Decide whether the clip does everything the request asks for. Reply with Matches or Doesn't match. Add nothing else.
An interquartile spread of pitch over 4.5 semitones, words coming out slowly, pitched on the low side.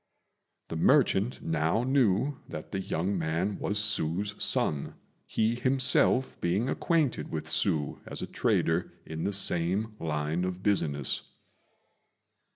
Matches